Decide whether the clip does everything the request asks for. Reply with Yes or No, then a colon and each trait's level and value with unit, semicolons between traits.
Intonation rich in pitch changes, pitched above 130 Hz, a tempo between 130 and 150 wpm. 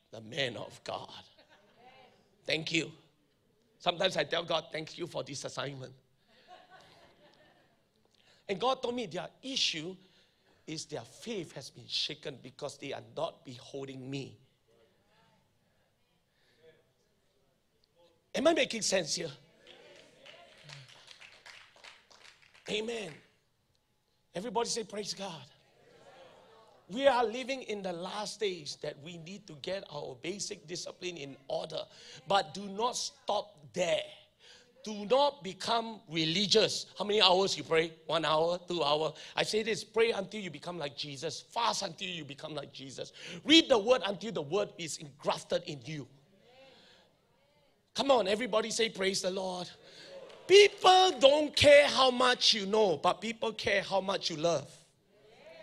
Yes: wide, 6.2 semitones; high, 190 Hz; slow, 135 wpm